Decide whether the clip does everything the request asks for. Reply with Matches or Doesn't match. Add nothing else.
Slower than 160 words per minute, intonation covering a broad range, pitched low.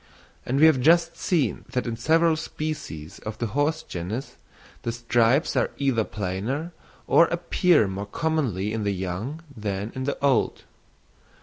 Matches